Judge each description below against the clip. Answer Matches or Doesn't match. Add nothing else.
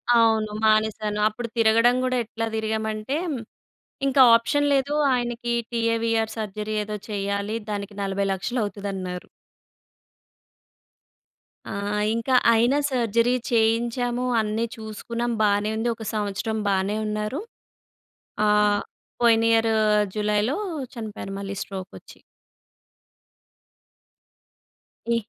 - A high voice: Matches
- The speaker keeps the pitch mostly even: Matches